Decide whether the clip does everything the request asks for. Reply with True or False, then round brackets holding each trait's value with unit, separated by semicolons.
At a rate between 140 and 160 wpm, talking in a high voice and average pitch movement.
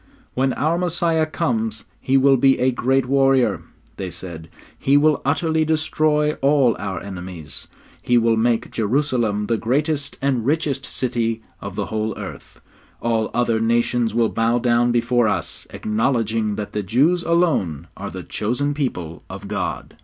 False (155 wpm; 120 Hz; 4.3 semitones)